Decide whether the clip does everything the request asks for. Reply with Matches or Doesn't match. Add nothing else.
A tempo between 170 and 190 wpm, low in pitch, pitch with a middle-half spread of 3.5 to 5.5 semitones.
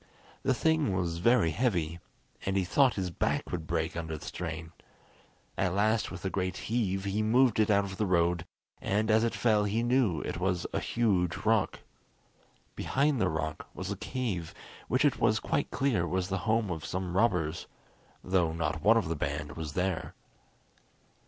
Matches